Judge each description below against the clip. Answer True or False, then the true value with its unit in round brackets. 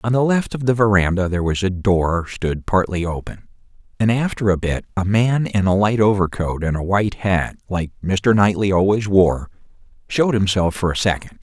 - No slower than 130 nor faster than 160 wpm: False (195 wpm)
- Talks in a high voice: False (100 Hz)